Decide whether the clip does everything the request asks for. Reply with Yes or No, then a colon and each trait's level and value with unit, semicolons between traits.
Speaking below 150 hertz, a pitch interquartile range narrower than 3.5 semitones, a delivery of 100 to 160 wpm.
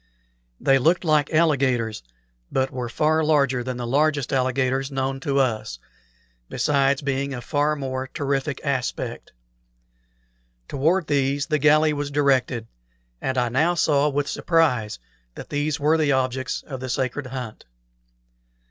Yes: medium, 140 Hz; narrow, 2.4 semitones; average, 140 wpm